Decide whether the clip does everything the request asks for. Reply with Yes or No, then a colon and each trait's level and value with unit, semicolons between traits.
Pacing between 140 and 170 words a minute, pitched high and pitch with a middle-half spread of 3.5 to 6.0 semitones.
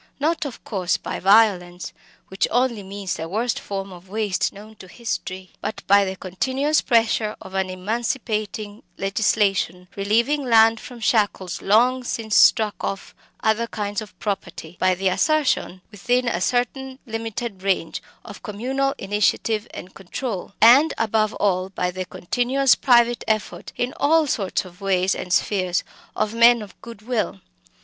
Yes: average, 150 wpm; high, 215 Hz; average, 3.8 semitones